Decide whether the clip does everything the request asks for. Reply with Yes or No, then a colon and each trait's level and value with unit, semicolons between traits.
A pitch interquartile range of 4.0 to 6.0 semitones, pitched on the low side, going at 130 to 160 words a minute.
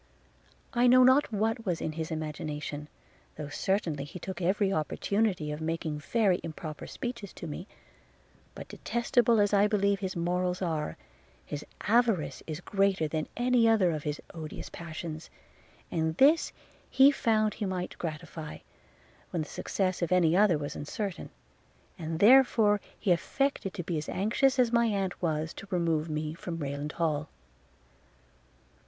No: average, 5.1 semitones; medium, 180 Hz; average, 155 wpm